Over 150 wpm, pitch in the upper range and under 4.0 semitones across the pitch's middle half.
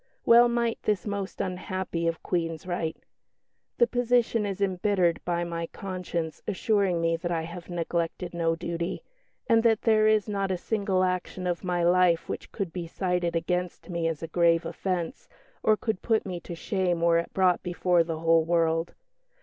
No: average, 175 wpm; medium, 180 Hz; average, 2.9 semitones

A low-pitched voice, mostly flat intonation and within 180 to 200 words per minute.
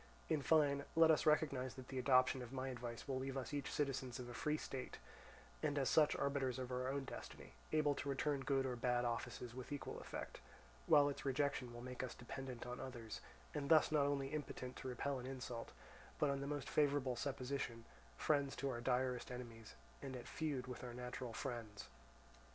Yes: low, 130 Hz; narrow, 2.3 semitones; average, 195 wpm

